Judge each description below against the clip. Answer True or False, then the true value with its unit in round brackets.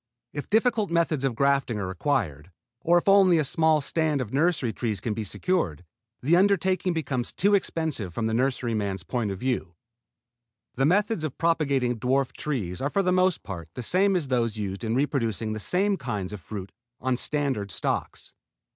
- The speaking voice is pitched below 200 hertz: True (135 Hz)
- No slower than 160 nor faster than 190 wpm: True (180 wpm)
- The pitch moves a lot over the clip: True (7.5 semitones)